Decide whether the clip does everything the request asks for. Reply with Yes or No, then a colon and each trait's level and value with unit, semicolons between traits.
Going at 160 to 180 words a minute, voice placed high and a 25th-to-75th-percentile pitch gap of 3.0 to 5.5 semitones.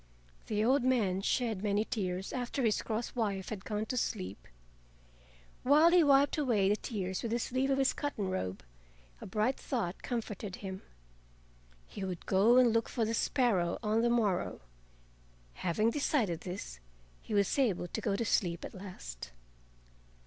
Yes: average, 165 wpm; high, 215 Hz; average, 4.4 semitones